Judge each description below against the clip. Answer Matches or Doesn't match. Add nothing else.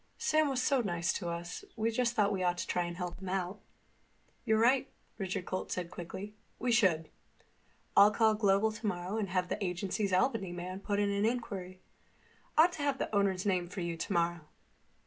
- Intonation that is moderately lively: Matches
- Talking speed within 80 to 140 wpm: Doesn't match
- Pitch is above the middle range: Matches